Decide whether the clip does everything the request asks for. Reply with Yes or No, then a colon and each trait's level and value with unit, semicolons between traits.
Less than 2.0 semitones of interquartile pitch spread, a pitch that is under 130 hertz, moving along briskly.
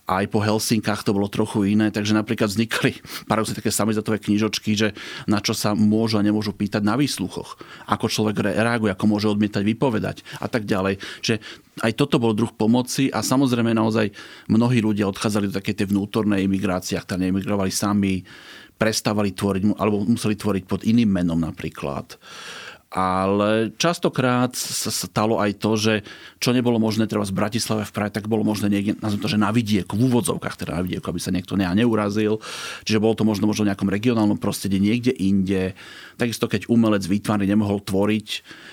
Yes: narrow, 1.6 semitones; low, 105 Hz; fast, 175 wpm